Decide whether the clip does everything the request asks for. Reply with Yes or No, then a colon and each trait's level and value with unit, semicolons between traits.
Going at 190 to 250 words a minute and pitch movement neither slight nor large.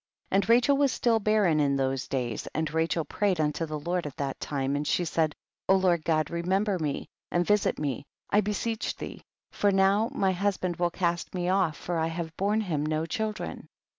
Yes: average, 200 wpm; average, 4.5 semitones